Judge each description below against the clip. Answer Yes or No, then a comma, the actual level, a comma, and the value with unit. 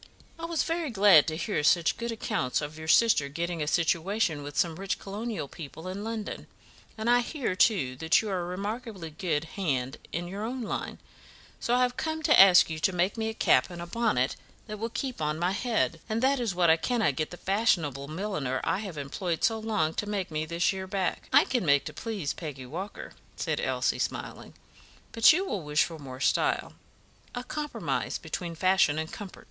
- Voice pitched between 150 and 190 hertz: Yes, medium, 185 Hz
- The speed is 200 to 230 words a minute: Yes, fast, 205 wpm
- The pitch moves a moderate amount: No, wide, 5.8 semitones